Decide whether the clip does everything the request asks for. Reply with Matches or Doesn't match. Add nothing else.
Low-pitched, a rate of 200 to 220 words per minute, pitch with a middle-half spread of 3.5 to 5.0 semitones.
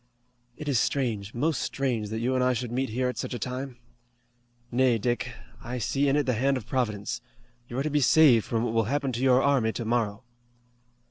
Doesn't match